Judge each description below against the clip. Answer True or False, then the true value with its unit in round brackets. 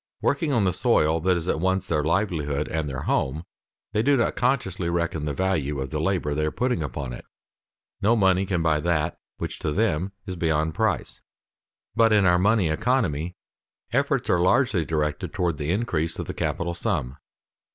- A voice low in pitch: True (85 Hz)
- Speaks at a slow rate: False (185 wpm)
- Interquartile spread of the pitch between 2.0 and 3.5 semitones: False (4.2 semitones)